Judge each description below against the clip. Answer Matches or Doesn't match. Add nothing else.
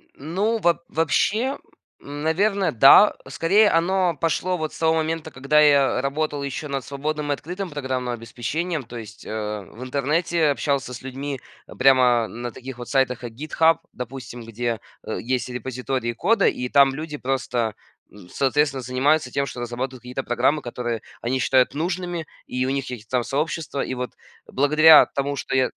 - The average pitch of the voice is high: Doesn't match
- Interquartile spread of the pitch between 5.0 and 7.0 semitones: Doesn't match